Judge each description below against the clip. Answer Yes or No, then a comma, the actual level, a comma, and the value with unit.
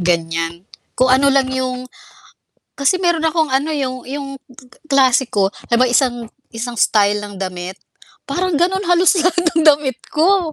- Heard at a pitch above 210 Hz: Yes, very high, 265 Hz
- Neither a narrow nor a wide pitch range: No, wide, 5.9 semitones